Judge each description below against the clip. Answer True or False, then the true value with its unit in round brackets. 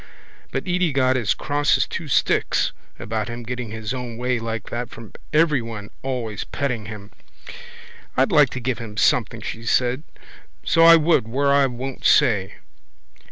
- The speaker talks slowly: False (160 wpm)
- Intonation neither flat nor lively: True (3.5 semitones)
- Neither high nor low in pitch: False (125 Hz)